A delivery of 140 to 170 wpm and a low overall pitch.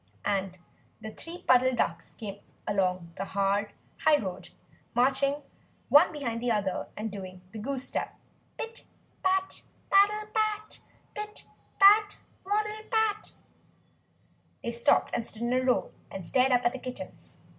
No: average, 145 wpm; very high, 255 Hz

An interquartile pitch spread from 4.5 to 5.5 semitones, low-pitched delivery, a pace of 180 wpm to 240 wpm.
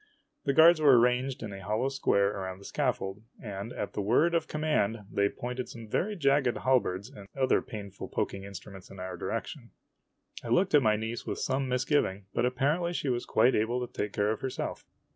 Yes: average, 5.2 semitones; low, 120 Hz; average, 200 wpm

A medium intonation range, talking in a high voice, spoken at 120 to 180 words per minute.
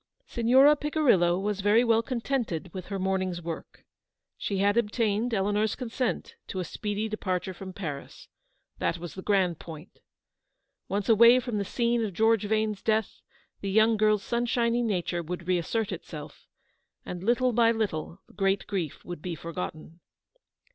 Yes: average, 4.0 semitones; high, 205 Hz; average, 155 wpm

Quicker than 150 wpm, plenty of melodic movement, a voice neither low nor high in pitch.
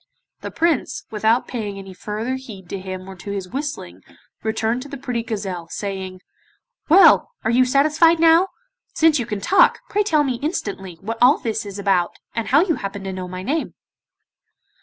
No: average, 180 wpm; wide, 6.6 semitones; high, 225 Hz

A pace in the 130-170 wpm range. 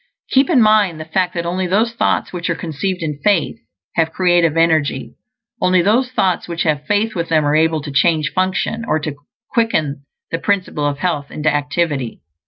No: average, 190 wpm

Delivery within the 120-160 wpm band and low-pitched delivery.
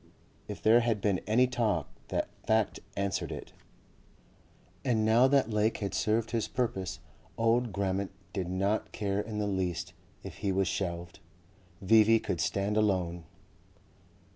Yes: average, 140 wpm; low, 105 Hz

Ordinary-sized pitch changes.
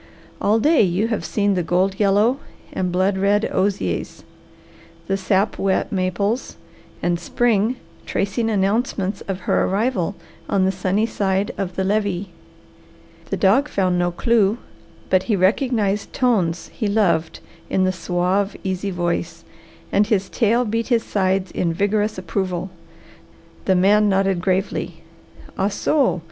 No: narrow, 2.3 semitones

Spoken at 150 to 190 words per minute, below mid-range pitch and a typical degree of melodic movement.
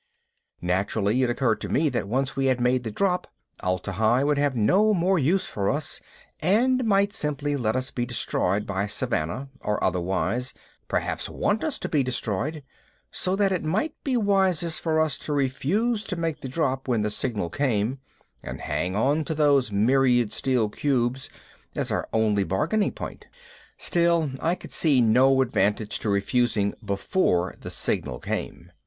No: average, 165 wpm; low, 130 Hz; wide, 7.0 semitones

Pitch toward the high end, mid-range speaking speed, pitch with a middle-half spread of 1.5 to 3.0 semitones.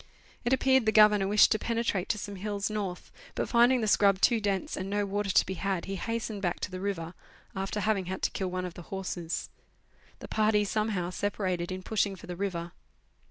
No: high, 200 Hz; fast, 215 wpm; narrow, 2.4 semitones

